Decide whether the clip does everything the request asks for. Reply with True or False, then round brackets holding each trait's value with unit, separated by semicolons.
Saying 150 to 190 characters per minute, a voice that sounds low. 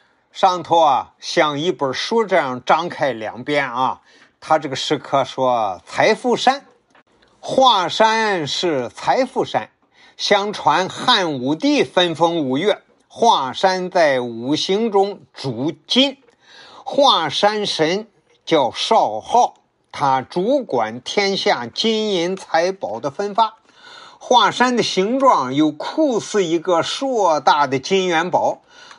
False (165 characters per minute; 190 Hz)